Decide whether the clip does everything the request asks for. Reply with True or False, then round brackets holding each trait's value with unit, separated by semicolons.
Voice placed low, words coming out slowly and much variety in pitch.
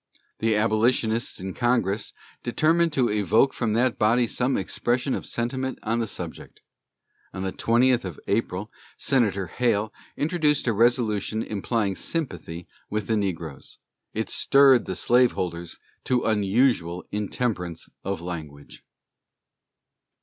False (110 Hz; 120 wpm; 4.4 semitones)